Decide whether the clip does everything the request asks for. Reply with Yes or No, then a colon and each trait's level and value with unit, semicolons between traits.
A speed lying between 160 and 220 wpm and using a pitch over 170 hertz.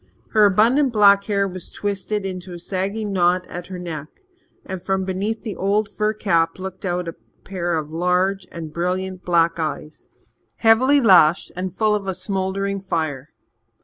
Yes: average, 165 wpm; high, 190 Hz